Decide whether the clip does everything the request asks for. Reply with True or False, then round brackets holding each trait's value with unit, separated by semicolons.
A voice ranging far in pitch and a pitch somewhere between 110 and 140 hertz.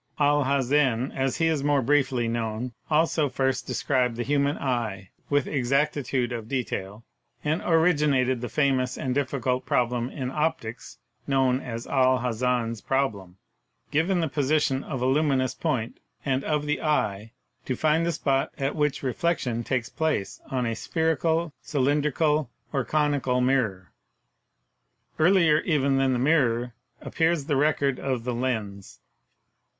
False (3.3 semitones; 135 Hz)